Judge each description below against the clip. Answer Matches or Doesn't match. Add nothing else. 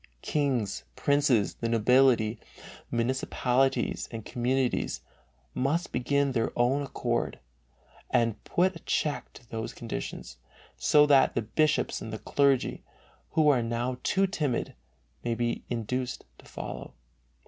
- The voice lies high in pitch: Doesn't match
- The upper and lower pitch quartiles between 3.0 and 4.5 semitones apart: Matches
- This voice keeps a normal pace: Doesn't match